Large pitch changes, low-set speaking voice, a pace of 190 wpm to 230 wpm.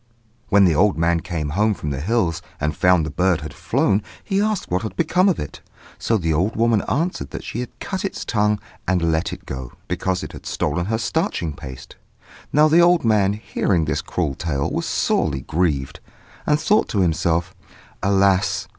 Yes: wide, 5.8 semitones; very low, 95 Hz; average, 195 wpm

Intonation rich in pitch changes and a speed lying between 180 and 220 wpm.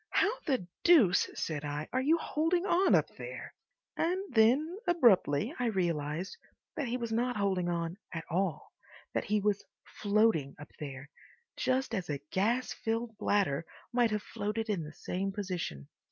No: wide, 6.7 semitones; average, 155 wpm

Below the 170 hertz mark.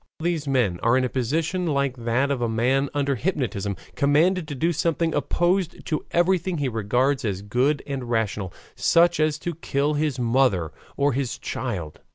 Yes: medium, 140 Hz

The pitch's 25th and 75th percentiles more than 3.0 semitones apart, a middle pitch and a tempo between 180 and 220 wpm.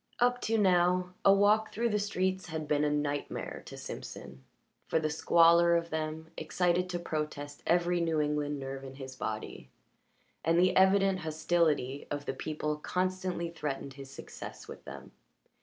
No: average, 3.7 semitones; medium, 165 Hz; average, 165 wpm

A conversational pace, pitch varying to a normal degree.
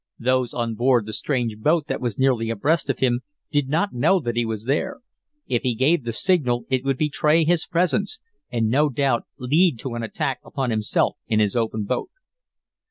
Yes: average, 195 wpm; average, 4.5 semitones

